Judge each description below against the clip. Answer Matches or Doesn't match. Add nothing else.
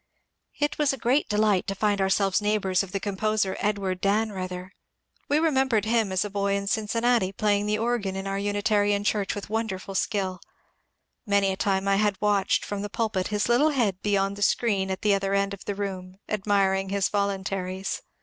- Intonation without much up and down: Matches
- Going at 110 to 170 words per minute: Doesn't match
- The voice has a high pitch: Matches